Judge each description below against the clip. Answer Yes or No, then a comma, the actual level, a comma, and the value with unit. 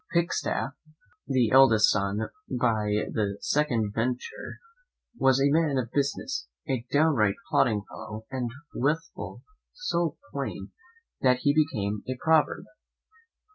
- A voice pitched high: No, low, 130 Hz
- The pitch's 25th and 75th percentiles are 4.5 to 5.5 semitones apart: Yes, average, 5.2 semitones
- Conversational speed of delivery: No, slow, 115 wpm